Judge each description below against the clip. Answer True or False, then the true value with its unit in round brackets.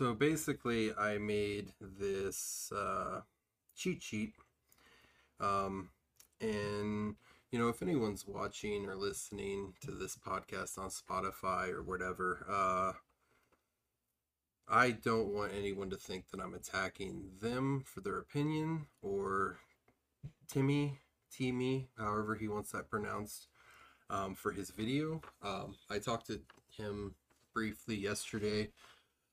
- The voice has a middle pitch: False (105 Hz)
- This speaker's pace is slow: True (115 wpm)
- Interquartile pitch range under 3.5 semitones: False (3.8 semitones)